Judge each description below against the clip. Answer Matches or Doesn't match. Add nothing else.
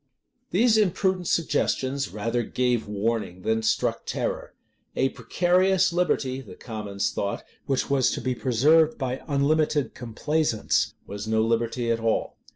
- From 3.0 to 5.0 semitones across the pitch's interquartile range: Doesn't match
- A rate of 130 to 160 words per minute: Matches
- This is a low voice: Matches